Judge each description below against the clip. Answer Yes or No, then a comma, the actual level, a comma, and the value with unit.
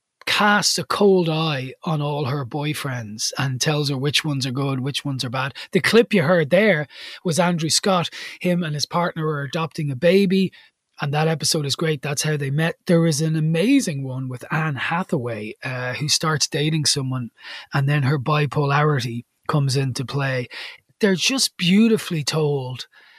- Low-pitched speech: No, medium, 155 Hz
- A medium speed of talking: Yes, average, 175 wpm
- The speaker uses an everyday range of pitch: Yes, average, 3.8 semitones